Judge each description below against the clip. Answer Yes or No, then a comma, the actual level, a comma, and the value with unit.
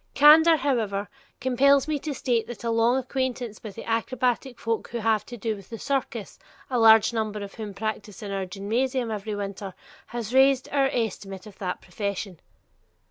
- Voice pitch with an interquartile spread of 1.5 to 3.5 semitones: No, average, 3.9 semitones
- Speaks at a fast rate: No, average, 180 wpm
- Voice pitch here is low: No, high, 225 Hz